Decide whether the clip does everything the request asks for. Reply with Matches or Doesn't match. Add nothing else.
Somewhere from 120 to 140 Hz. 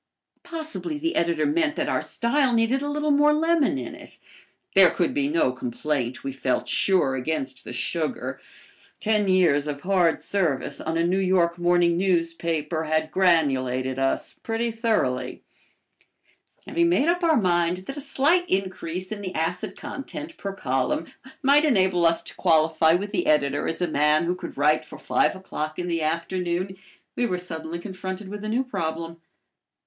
Doesn't match